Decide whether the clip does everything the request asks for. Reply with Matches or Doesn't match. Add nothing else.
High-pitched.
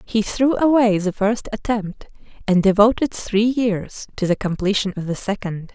Matches